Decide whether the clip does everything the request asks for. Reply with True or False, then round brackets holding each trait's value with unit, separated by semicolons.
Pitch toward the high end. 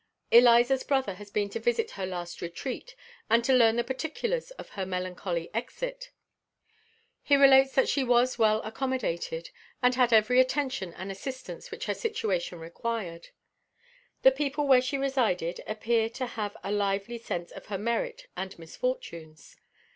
True (235 Hz)